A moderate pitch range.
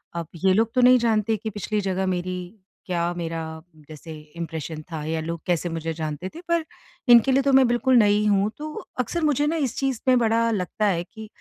No: wide, 5.9 semitones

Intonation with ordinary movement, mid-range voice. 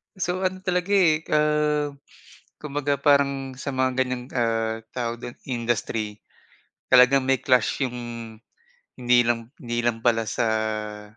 No: average, 3.9 semitones; low, 125 Hz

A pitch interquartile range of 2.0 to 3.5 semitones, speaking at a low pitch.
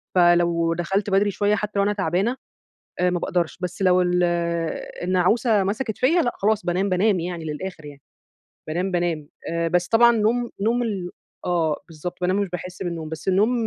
No: average, 3.0 semitones; medium, 180 Hz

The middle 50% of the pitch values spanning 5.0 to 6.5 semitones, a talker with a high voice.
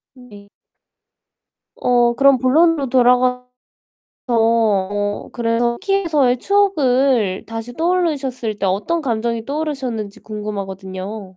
No: average, 4.5 semitones; high, 240 Hz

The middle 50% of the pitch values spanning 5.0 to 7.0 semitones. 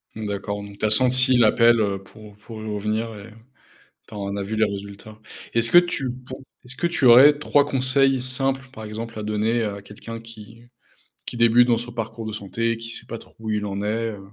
No: average, 2.7 semitones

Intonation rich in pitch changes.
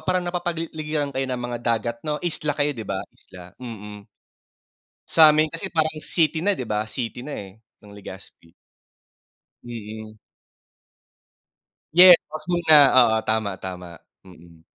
Yes: wide, 7.0 semitones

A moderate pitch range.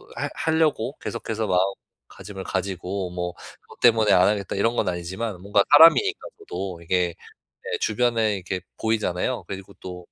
Yes: average, 3.8 semitones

